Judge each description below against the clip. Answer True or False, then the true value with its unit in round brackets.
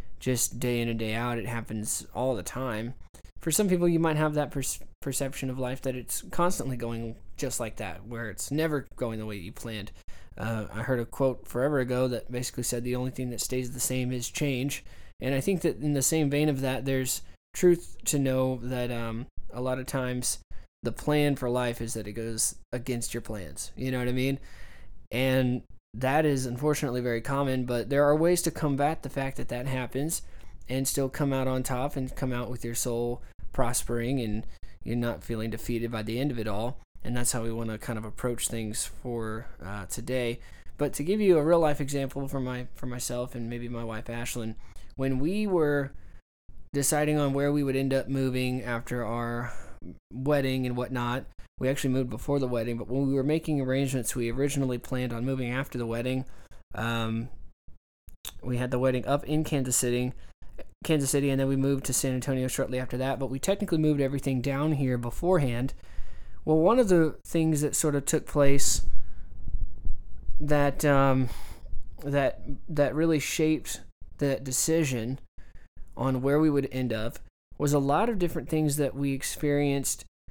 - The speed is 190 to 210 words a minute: True (195 wpm)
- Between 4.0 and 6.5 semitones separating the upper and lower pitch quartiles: False (3.3 semitones)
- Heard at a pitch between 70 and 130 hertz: True (125 Hz)